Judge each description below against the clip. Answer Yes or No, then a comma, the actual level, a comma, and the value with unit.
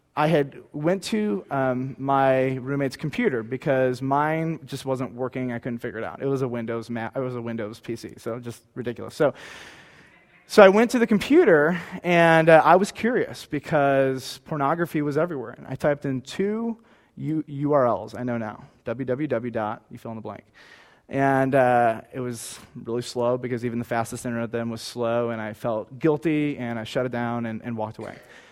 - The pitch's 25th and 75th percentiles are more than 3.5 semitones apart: Yes, average, 3.9 semitones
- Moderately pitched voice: No, low, 130 Hz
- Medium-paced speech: Yes, average, 190 wpm